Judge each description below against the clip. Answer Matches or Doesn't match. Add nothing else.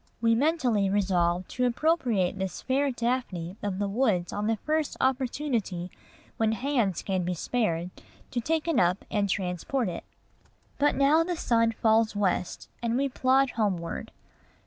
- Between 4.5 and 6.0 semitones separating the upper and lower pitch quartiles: Matches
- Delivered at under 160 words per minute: Matches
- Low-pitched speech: Doesn't match